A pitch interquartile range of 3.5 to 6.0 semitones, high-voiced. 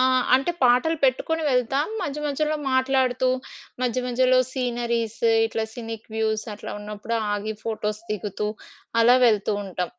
No: average, 3.1 semitones; high, 240 Hz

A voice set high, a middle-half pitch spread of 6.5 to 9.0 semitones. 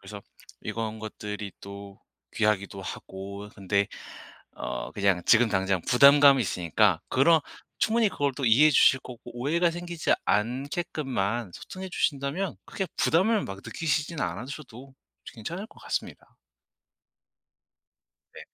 No: low, 120 Hz; wide, 7.3 semitones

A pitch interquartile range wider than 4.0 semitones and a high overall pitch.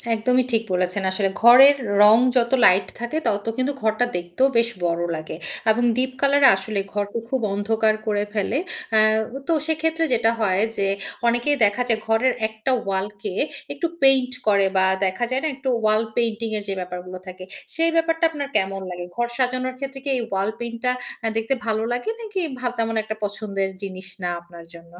Yes: average, 4.5 semitones; high, 220 Hz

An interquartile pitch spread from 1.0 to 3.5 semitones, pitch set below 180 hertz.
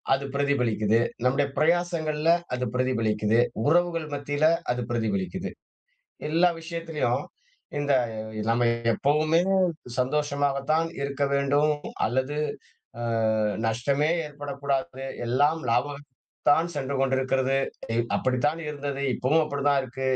Yes: average, 2.8 semitones; medium, 140 Hz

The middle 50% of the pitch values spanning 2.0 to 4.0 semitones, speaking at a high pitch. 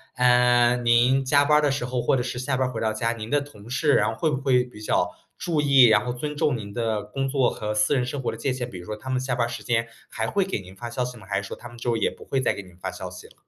No: average, 3.1 semitones; low, 125 Hz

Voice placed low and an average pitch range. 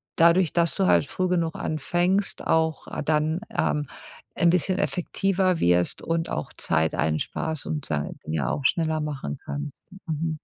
No: medium, 160 Hz; average, 3.4 semitones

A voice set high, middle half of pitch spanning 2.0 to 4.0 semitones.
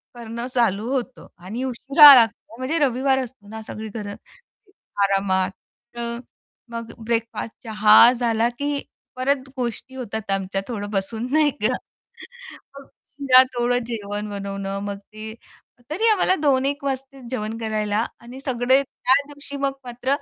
Yes: high, 235 Hz; average, 3.7 semitones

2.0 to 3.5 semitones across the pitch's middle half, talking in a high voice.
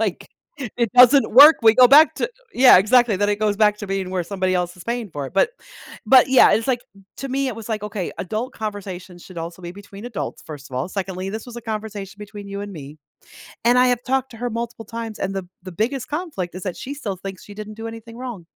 No: average, 4.2 semitones; high, 215 Hz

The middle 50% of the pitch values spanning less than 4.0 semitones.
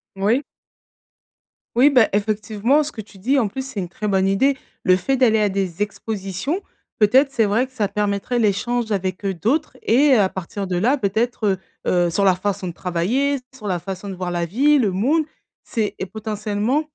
No: average, 4.6 semitones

